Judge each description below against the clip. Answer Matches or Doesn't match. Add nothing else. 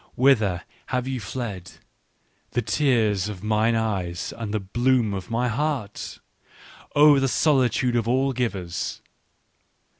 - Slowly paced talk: Matches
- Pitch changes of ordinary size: Matches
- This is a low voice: Matches